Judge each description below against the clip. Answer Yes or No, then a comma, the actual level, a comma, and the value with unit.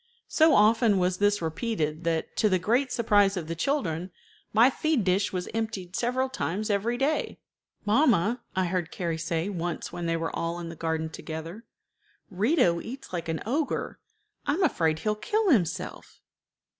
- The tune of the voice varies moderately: No, wide, 5.9 semitones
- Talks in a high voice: Yes, high, 195 Hz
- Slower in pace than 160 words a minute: No, average, 170 wpm